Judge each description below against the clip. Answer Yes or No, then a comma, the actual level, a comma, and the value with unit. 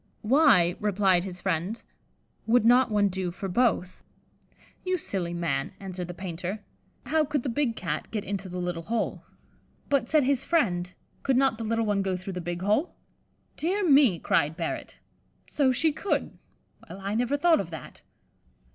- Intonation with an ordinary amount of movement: No, wide, 6.5 semitones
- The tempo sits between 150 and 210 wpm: Yes, average, 170 wpm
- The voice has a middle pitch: No, high, 205 Hz